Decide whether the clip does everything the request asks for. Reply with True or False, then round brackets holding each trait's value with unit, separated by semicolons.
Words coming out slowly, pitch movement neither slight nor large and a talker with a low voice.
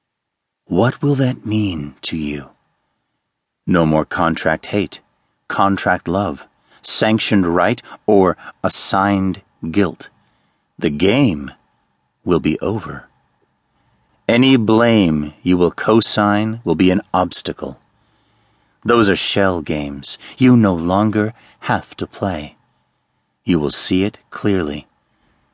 True (110 wpm; 4.8 semitones; 95 Hz)